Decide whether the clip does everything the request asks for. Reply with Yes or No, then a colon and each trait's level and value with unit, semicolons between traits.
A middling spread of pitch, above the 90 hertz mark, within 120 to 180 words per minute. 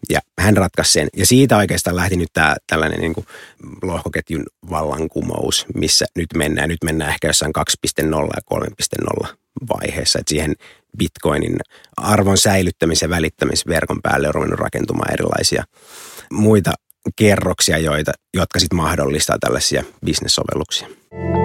No: average, 3.3 semitones; very low, 85 Hz; average, 130 wpm